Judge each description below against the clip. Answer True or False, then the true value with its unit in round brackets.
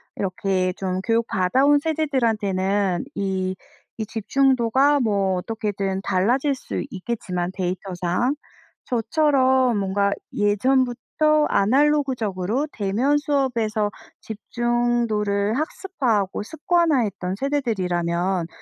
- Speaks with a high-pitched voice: True (220 Hz)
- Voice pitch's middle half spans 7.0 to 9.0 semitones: False (5.5 semitones)